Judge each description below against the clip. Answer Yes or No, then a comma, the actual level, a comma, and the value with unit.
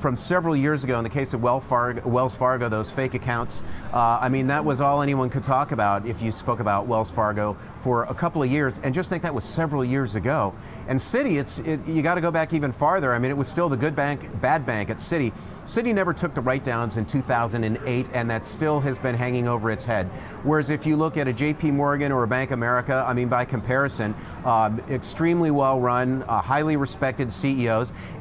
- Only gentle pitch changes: No, average, 3.6 semitones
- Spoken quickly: Yes, fast, 225 wpm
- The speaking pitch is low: Yes, low, 130 Hz